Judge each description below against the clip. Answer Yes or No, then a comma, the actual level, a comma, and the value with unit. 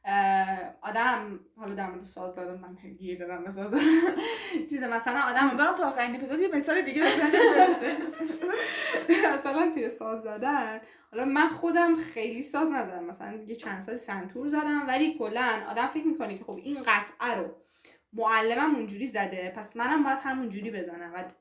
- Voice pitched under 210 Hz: No, very high, 250 Hz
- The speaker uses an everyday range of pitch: No, wide, 7.4 semitones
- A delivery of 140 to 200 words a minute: Yes, fast, 155 wpm